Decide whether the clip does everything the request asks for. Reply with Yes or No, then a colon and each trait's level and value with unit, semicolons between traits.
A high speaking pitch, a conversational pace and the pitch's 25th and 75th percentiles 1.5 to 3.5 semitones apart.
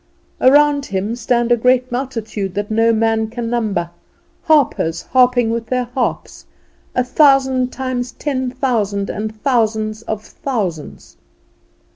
No: high, 240 Hz; slow, 125 wpm; average, 2.9 semitones